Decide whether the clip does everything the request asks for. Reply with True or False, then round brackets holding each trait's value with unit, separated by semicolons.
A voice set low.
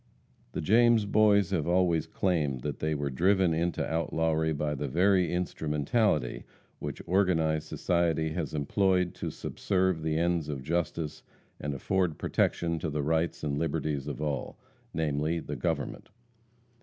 True (80 Hz)